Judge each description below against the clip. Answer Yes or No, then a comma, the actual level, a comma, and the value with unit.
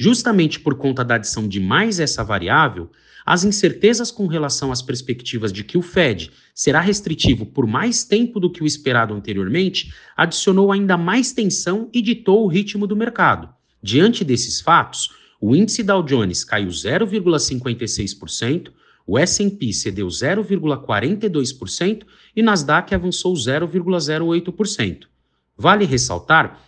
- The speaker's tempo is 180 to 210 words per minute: No, average, 130 wpm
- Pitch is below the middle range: No, medium, 170 Hz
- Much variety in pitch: Yes, wide, 8.7 semitones